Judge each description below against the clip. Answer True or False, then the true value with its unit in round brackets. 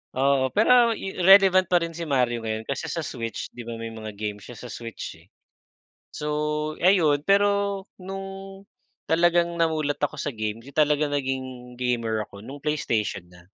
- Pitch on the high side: False (145 Hz)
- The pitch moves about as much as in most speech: False (6.8 semitones)